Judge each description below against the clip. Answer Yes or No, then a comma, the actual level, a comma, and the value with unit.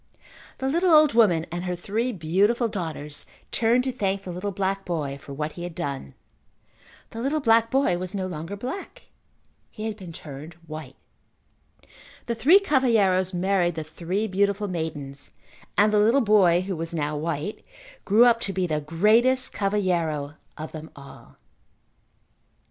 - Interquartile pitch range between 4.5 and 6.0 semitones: Yes, wide, 5.6 semitones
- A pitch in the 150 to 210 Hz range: Yes, high, 190 Hz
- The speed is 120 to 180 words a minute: Yes, average, 160 wpm